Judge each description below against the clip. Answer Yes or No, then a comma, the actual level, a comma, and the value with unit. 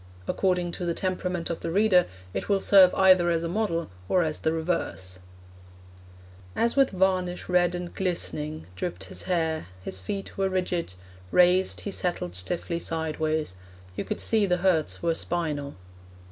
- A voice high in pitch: No, medium, 175 Hz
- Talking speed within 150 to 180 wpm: Yes, average, 160 wpm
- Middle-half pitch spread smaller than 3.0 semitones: Yes, narrow, 2.5 semitones